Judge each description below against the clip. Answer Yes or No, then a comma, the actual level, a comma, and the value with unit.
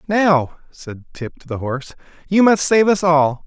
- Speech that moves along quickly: No, average, 190 wpm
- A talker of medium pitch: Yes, medium, 165 Hz